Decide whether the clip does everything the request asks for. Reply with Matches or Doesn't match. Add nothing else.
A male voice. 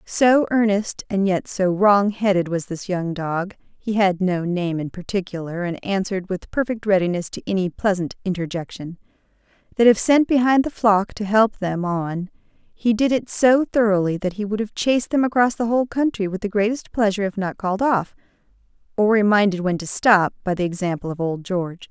Doesn't match